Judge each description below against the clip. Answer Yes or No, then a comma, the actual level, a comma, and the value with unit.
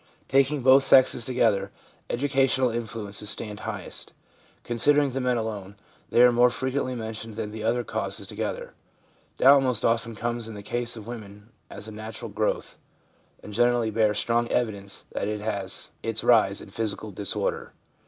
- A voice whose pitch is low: Yes, low, 115 Hz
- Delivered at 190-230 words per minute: No, average, 165 wpm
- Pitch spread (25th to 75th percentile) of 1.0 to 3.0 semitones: Yes, average, 2.7 semitones